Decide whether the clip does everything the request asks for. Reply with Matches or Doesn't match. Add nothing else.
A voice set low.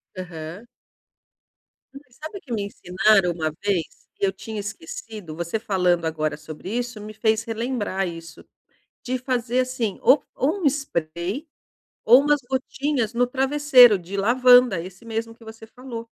Doesn't match